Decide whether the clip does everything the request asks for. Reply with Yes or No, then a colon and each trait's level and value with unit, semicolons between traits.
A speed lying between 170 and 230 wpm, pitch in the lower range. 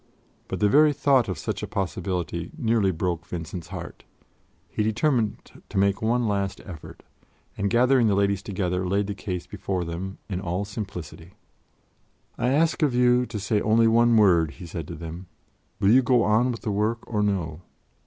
Yes: average, 180 wpm; low, 100 Hz